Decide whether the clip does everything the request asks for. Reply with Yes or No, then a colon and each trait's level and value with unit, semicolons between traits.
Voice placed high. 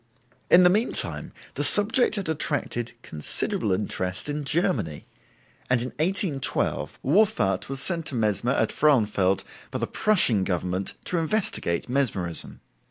No: low, 135 Hz